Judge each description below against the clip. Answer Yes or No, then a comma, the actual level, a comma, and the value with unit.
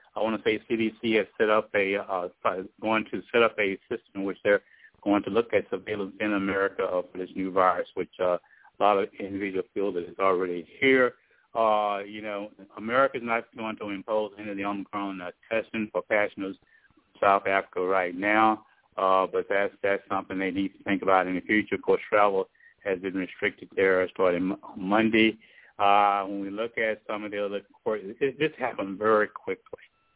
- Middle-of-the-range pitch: No, low, 100 Hz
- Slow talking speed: No, average, 185 wpm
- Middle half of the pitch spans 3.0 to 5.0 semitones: No, narrow, 2.4 semitones